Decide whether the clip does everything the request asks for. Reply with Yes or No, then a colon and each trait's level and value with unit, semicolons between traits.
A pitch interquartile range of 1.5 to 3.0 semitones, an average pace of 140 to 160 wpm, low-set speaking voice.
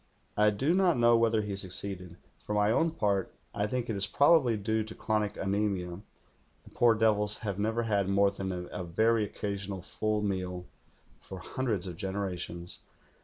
No: narrow, 2.5 semitones; average, 185 wpm; low, 105 Hz